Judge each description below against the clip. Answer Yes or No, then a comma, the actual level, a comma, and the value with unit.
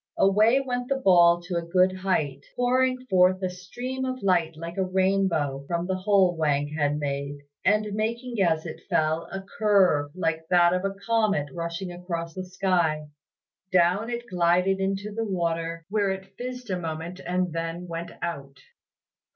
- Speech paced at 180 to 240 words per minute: No, average, 165 wpm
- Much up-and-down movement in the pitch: No, average, 3.1 semitones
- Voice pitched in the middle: Yes, medium, 180 Hz